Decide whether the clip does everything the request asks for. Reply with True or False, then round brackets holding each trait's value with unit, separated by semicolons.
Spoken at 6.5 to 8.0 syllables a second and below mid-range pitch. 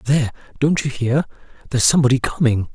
True (6.7 syllables/s; 130 Hz)